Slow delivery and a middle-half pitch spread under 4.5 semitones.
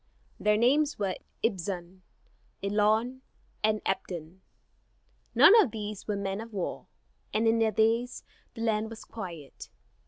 Yes: slow, 130 wpm; average, 2.7 semitones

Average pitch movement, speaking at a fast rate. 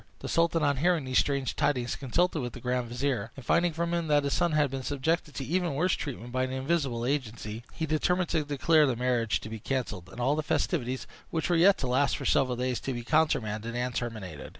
Yes: average, 4.5 semitones; fast, 230 wpm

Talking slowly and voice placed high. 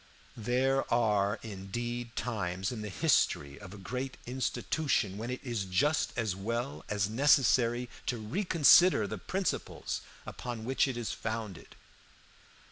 No: slow, 130 wpm; low, 115 Hz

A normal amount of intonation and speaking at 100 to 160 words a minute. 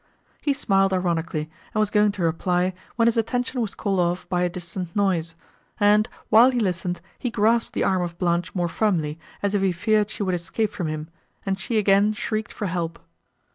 No: average, 3.5 semitones; average, 200 wpm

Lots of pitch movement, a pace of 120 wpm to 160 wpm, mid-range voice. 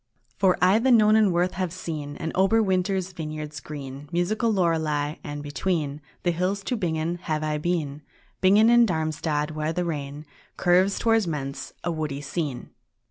No: average, 3.9 semitones; average, 155 wpm; medium, 170 Hz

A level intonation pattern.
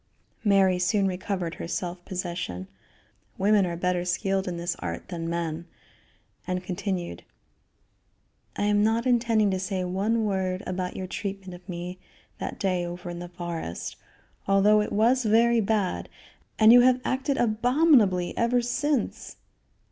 No: average, 3.5 semitones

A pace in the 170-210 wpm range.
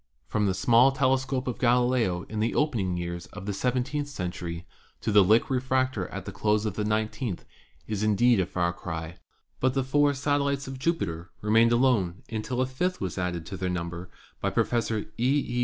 Yes: average, 190 wpm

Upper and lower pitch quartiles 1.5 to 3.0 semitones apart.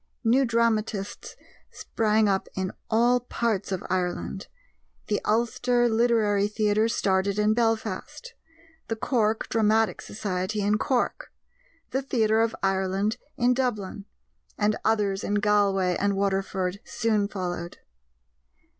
Yes: narrow, 2.6 semitones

